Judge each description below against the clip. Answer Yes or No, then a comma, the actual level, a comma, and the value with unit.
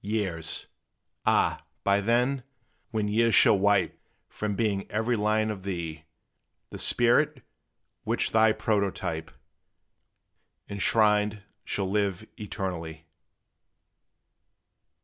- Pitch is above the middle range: No, low, 105 Hz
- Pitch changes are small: Yes, narrow, 2.3 semitones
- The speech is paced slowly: Yes, slow, 90 wpm